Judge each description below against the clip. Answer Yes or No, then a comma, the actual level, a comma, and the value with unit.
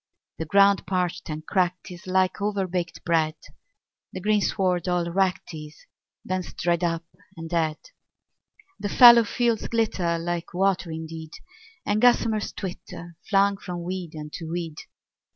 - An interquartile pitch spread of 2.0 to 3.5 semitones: Yes, average, 2.8 semitones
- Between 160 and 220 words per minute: No, slow, 135 wpm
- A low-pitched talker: No, medium, 180 Hz